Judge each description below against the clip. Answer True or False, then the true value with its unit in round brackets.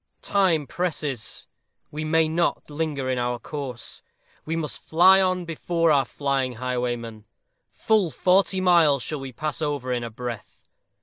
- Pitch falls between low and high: True (150 Hz)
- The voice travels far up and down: False (4.8 semitones)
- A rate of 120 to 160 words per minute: True (150 wpm)